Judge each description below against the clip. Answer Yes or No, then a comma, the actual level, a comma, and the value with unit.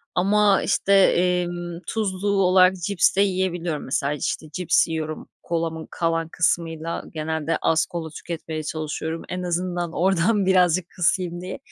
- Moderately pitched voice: Yes, medium, 175 Hz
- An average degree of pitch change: No, narrow, 2.3 semitones